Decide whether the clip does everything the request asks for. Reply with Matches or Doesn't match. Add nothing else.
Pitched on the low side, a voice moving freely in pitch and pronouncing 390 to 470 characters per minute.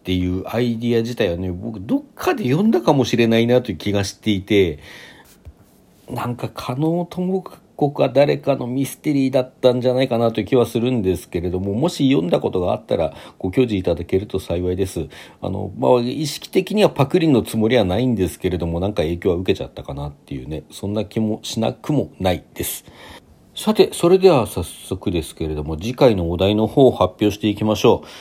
Matches